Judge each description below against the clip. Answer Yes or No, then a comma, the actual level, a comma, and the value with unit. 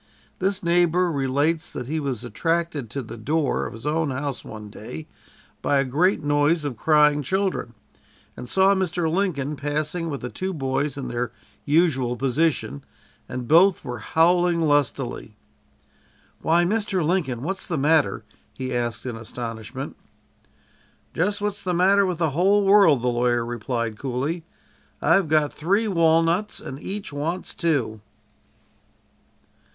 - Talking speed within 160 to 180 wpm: No, average, 145 wpm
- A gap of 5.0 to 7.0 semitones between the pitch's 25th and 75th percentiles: Yes, wide, 5.4 semitones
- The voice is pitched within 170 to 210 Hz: No, medium, 150 Hz